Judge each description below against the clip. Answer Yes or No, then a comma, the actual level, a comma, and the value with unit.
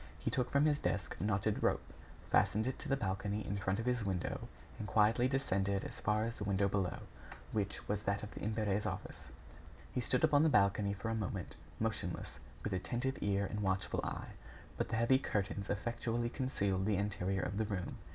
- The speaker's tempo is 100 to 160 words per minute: No, average, 200 wpm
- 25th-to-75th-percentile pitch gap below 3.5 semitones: Yes, average, 3.1 semitones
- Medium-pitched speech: No, low, 105 Hz